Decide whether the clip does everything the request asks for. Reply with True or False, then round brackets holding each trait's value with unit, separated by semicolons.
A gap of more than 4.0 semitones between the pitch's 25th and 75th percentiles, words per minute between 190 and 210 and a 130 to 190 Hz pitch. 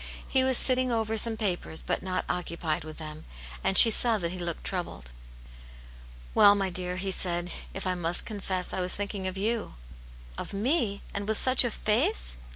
True (4.4 semitones; 200 wpm; 185 Hz)